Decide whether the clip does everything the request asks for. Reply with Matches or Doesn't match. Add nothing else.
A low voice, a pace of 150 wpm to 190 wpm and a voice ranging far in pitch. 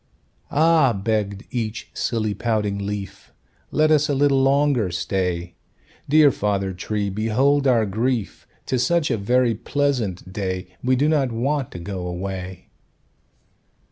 Doesn't match